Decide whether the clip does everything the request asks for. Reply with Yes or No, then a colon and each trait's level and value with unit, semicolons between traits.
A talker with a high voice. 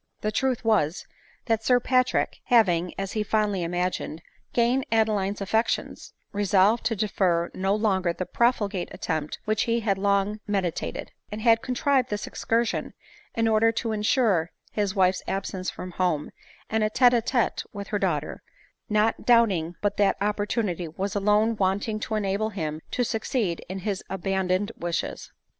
Yes: high, 205 Hz